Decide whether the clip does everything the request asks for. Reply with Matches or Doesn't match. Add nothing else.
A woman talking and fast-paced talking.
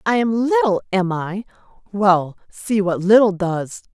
Doesn't match